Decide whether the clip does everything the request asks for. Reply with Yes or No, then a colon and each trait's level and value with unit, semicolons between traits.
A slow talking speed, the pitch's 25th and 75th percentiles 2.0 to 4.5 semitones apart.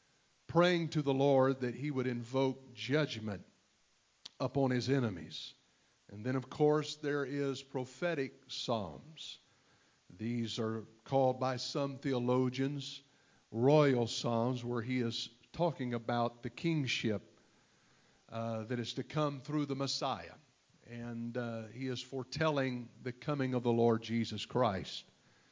Yes: slow, 130 wpm; average, 2.8 semitones